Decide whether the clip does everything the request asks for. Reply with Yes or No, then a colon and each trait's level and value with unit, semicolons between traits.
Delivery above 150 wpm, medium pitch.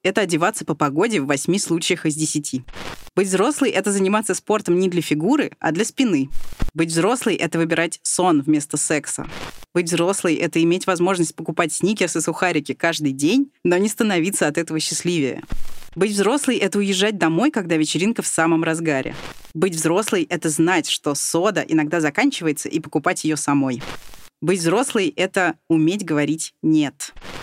Yes: fast, 160 wpm; medium, 170 Hz